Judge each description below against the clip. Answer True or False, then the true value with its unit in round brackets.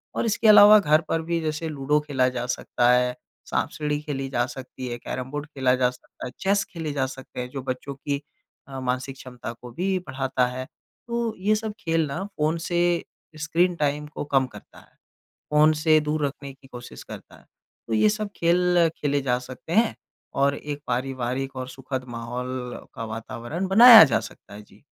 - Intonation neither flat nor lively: True (4.3 semitones)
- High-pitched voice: False (140 Hz)